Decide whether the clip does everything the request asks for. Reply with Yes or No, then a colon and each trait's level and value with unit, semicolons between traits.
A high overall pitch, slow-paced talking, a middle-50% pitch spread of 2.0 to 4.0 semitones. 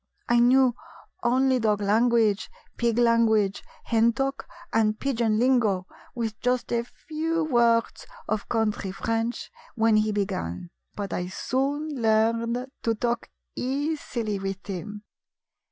Yes: high, 230 Hz; slow, 125 wpm; average, 2.7 semitones